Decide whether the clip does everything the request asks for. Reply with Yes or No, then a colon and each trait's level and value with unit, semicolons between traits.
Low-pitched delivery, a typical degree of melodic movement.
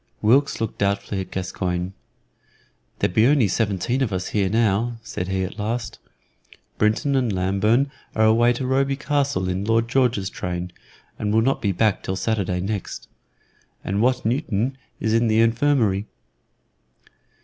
Yes: low, 110 Hz; average, 4.0 semitones